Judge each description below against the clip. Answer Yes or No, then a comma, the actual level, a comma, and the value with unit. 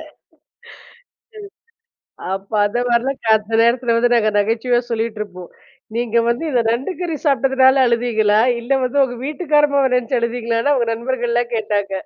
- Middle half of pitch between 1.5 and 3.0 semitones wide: Yes, narrow, 2.4 semitones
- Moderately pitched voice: No, high, 240 Hz